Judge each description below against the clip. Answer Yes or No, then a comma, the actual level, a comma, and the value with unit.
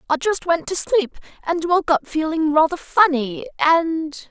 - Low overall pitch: No, very high, 320 Hz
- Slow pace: No, average, 165 wpm